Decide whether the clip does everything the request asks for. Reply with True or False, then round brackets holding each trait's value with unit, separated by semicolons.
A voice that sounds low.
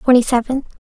False (255 Hz)